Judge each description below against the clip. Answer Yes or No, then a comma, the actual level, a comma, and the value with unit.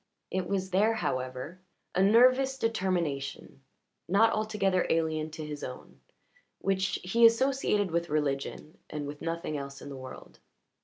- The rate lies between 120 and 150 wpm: Yes, average, 140 wpm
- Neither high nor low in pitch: Yes, medium, 180 Hz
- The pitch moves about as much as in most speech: No, wide, 6.1 semitones